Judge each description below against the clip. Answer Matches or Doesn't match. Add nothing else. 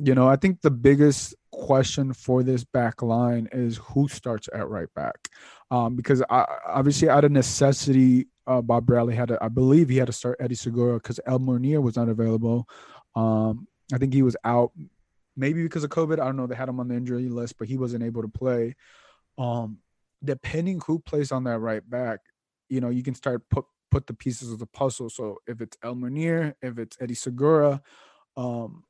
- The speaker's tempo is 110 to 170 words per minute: Doesn't match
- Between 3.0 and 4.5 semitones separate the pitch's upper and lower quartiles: Doesn't match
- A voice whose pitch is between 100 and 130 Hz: Matches